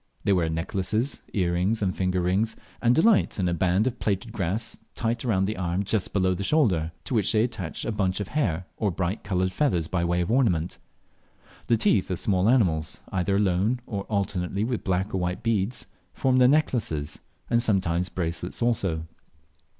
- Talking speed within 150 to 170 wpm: No, average, 180 wpm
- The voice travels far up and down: No, average, 4.1 semitones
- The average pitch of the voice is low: Yes, very low, 95 Hz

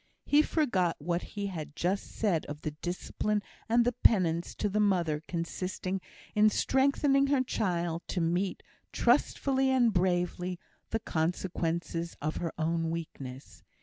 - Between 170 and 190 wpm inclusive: No, slow, 135 wpm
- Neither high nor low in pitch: Yes, medium, 180 Hz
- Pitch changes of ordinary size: Yes, average, 4.2 semitones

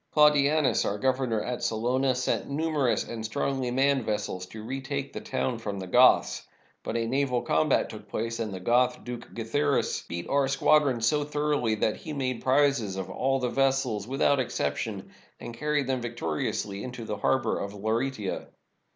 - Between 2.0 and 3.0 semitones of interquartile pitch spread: No, average, 3.7 semitones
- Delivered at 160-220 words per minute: Yes, average, 170 wpm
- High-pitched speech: No, low, 125 Hz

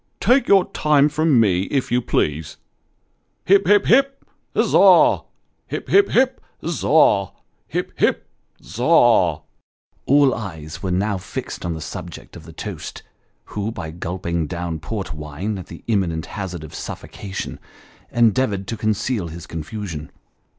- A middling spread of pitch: No, wide, 7.7 semitones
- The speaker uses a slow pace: No, average, 145 wpm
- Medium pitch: No, low, 100 Hz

